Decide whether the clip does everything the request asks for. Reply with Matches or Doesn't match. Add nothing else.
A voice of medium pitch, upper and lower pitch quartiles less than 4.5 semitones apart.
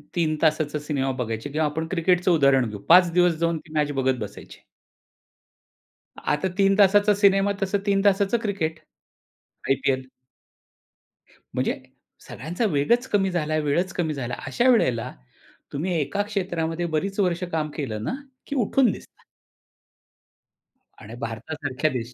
Doesn't match